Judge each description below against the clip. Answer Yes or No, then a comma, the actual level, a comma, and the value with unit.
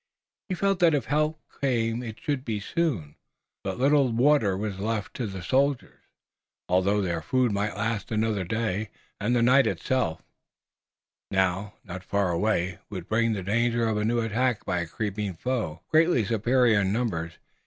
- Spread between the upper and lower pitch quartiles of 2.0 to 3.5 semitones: No, average, 4.5 semitones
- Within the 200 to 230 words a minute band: No, average, 165 wpm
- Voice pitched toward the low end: Yes, low, 110 Hz